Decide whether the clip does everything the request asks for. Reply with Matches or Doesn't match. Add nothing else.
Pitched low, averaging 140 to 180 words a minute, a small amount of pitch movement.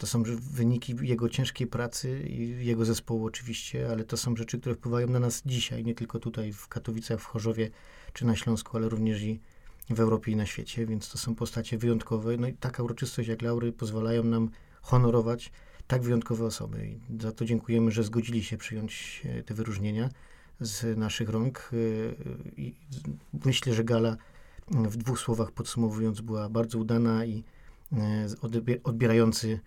Matches